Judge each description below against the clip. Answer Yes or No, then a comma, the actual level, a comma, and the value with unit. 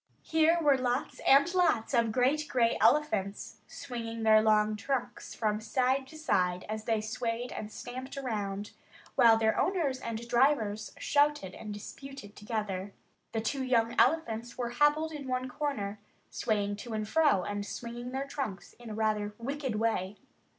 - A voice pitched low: No, high, 235 Hz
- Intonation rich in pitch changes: No, average, 4.3 semitones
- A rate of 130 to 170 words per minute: Yes, average, 155 wpm